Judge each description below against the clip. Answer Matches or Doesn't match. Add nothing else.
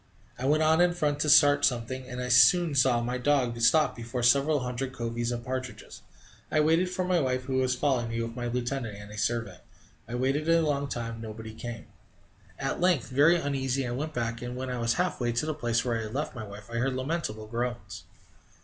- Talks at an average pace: Doesn't match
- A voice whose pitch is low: Matches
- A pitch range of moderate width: Matches